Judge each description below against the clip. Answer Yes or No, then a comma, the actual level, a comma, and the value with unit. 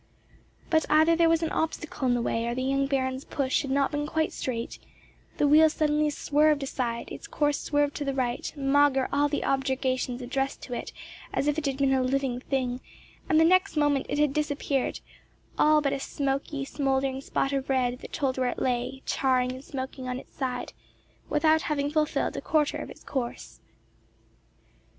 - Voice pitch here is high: Yes, very high, 275 Hz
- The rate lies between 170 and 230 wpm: Yes, average, 190 wpm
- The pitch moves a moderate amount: No, narrow, 2.2 semitones